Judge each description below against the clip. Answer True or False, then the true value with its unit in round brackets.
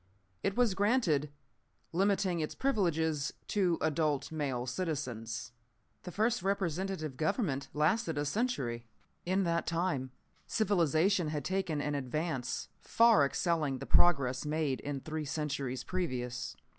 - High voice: False (160 Hz)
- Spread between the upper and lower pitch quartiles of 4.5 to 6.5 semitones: True (5.2 semitones)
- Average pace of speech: False (120 wpm)